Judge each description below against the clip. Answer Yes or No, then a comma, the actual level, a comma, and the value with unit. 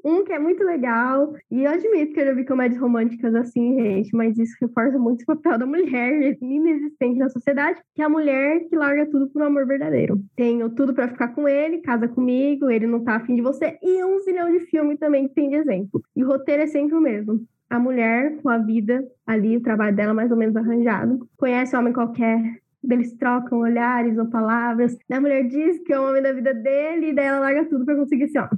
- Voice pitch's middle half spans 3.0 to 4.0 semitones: Yes, average, 3.7 semitones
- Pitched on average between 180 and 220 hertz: No, very high, 265 Hz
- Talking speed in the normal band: No, fast, 235 wpm